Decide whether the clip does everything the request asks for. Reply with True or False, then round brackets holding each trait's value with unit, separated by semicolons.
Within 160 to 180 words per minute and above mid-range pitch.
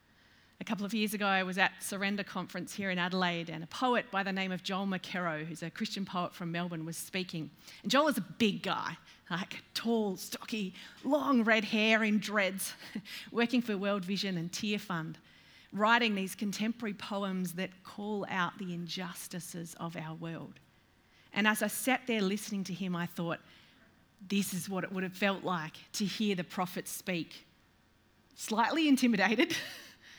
True (175 wpm; 195 Hz)